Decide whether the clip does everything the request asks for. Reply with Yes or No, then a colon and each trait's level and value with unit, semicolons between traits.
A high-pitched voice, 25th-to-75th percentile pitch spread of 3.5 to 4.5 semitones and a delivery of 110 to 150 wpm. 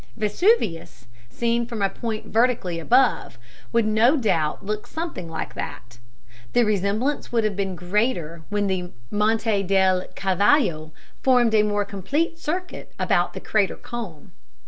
Yes: high, 210 Hz; average, 4.1 semitones; average, 140 wpm